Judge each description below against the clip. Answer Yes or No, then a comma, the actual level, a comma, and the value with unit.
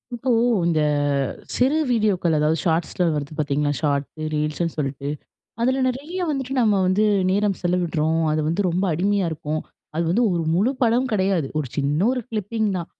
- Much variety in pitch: Yes, wide, 5.9 semitones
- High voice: No, medium, 175 Hz